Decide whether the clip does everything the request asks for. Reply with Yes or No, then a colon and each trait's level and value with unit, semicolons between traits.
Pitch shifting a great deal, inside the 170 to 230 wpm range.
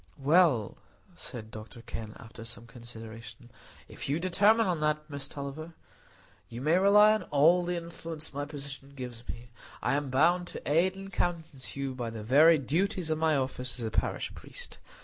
Yes: wide, 5.7 semitones; average, 175 wpm